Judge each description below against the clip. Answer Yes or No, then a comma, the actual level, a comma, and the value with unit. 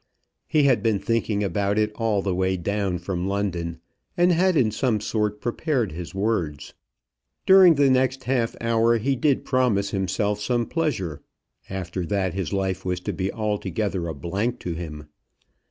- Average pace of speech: Yes, average, 165 wpm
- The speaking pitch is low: Yes, low, 105 Hz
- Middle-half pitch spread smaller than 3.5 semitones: No, average, 4.2 semitones